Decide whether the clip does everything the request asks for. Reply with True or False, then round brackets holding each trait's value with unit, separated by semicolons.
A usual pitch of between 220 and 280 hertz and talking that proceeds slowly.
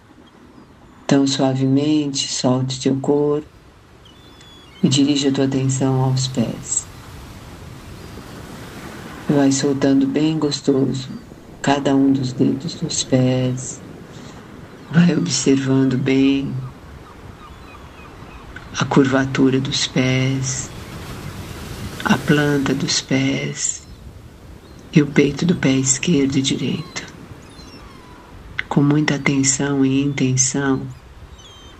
False (135 Hz; 85 wpm)